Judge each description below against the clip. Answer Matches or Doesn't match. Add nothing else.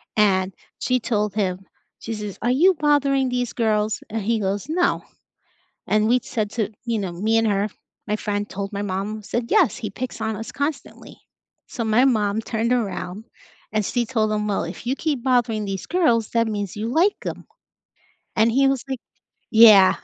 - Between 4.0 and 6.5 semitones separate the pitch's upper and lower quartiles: Doesn't match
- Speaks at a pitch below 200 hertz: Doesn't match